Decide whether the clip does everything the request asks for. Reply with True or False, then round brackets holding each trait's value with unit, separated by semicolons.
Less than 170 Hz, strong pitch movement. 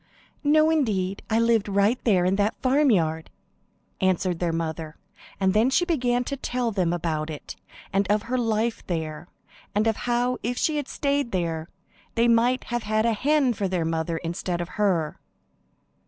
False (210 Hz; 5.9 semitones)